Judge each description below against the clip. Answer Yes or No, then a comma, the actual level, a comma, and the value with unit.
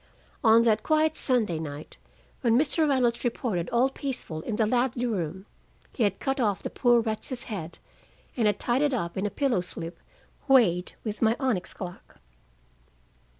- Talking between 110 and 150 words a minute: No, average, 165 wpm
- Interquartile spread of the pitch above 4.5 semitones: Yes, average, 5.3 semitones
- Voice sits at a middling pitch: No, high, 230 Hz